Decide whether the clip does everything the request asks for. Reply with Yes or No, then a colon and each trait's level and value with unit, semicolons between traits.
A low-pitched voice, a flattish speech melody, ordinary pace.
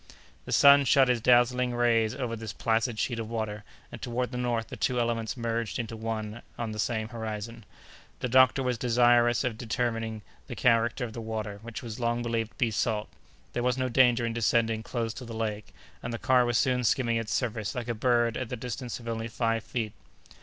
No: low, 115 Hz; narrow, 1.6 semitones; fast, 210 wpm